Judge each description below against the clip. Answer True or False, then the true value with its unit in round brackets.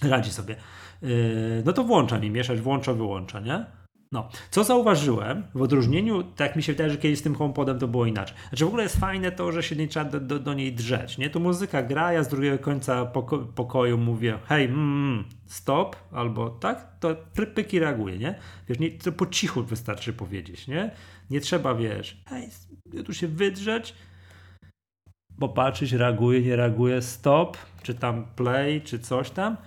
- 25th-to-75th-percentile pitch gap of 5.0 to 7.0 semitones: True (5.3 semitones)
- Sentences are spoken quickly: True (180 wpm)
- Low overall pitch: True (130 Hz)